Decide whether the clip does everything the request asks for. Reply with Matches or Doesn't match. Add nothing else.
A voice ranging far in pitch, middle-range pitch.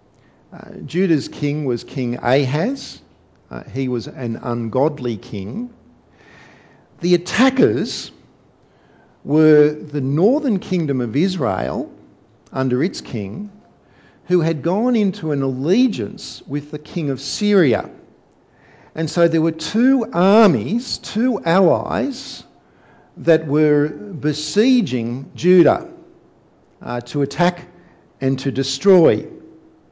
Matches